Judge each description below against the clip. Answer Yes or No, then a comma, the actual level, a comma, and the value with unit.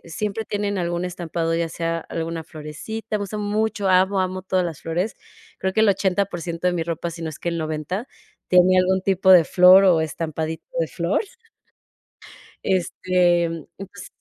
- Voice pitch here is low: No, medium, 180 Hz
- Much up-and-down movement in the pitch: No, narrow, 2.6 semitones